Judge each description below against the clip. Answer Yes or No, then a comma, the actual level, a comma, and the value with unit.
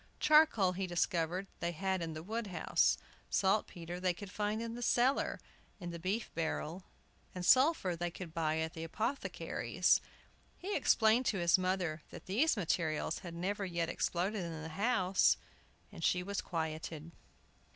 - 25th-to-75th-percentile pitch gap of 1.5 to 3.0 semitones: No, average, 3.8 semitones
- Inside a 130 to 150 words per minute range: No, average, 160 wpm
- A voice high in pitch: No, medium, 180 Hz